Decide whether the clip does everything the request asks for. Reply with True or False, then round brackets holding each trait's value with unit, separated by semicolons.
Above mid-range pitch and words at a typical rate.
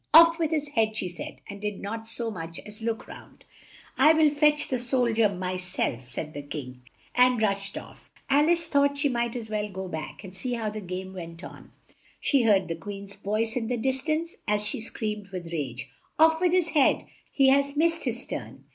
False (225 Hz; 210 wpm)